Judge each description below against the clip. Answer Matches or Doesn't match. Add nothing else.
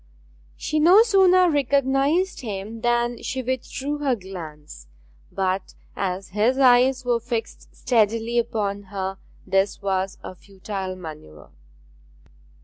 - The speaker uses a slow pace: Matches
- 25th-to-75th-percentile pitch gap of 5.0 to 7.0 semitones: Matches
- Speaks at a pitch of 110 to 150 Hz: Doesn't match